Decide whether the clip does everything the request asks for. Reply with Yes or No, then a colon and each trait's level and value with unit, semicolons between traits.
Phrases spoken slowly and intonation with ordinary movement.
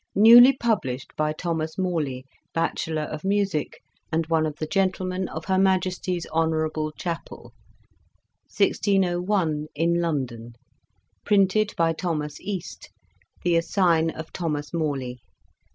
Yes: slow, 115 wpm; average, 3.4 semitones